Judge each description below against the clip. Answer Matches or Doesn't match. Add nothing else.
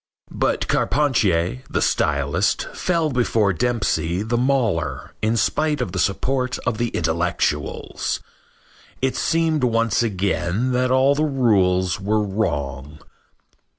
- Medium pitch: Doesn't match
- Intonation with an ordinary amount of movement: Doesn't match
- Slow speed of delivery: Matches